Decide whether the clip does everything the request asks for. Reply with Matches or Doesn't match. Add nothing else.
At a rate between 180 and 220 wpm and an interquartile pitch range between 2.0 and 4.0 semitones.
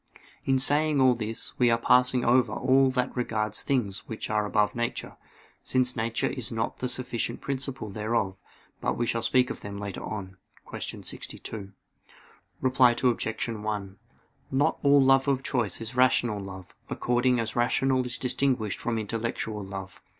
Doesn't match